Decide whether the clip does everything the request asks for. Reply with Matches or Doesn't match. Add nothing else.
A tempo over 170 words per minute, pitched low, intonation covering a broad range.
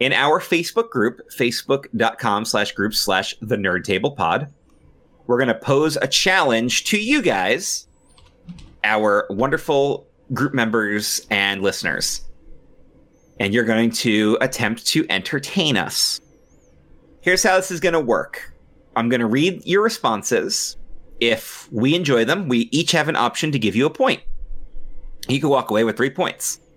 Doesn't match